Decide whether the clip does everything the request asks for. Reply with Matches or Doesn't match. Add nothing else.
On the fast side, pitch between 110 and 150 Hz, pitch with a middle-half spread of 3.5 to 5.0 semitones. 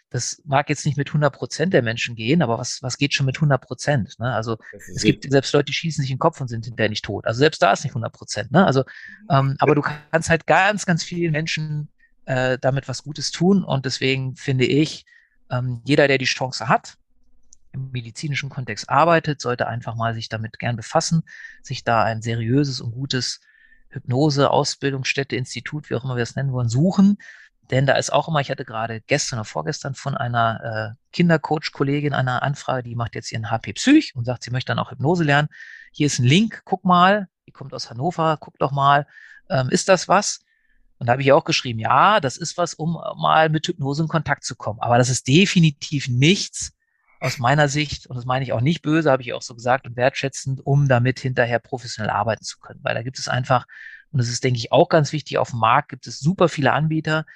Matches